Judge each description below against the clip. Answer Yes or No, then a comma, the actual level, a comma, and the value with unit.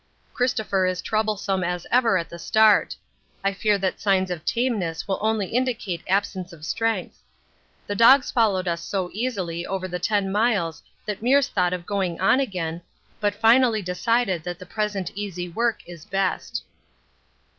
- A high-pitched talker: Yes, high, 195 Hz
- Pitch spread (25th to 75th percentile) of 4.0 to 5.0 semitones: No, average, 3.6 semitones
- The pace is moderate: Yes, average, 160 wpm